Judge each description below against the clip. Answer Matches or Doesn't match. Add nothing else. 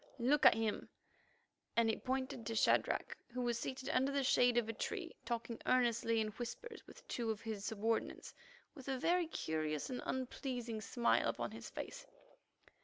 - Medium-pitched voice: Doesn't match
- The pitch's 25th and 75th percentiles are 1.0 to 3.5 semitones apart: Matches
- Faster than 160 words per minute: Matches